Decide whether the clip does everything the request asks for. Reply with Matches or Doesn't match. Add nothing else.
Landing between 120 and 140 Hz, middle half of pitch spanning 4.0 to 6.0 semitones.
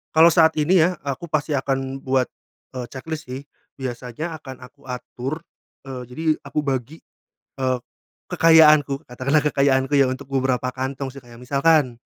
Doesn't match